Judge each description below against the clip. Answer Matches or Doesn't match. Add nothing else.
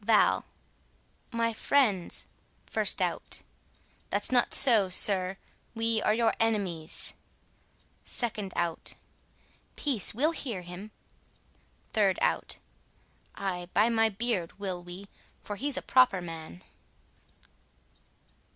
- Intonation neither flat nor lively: Matches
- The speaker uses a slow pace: Matches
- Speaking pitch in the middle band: Doesn't match